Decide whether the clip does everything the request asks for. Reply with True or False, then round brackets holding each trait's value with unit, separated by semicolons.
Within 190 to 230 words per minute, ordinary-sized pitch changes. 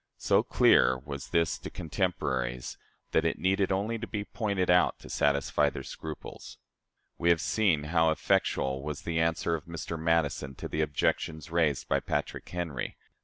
False (165 wpm; 3.4 semitones)